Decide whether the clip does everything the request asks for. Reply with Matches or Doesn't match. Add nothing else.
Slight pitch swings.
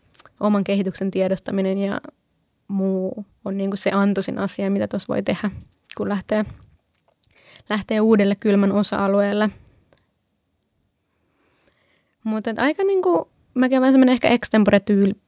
Matches